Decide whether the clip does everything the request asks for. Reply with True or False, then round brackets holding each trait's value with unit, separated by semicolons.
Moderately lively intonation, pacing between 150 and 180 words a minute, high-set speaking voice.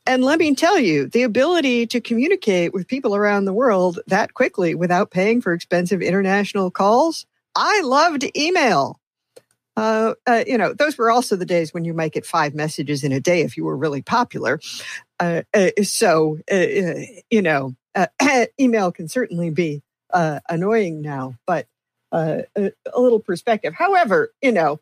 False (6.3 semitones; 170 wpm; 200 Hz)